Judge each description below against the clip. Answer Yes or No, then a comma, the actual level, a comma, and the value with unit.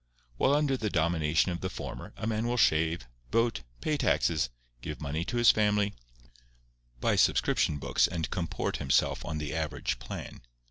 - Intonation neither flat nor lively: No, wide, 6.1 semitones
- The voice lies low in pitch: Yes, very low, 85 Hz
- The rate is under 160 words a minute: No, average, 165 wpm